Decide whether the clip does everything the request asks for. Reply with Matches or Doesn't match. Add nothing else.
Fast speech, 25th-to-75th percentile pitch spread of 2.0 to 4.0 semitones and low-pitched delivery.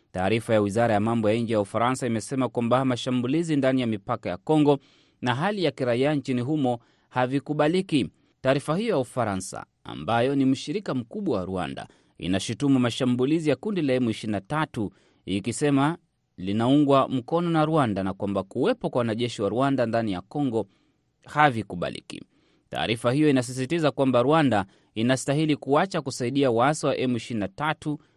Doesn't match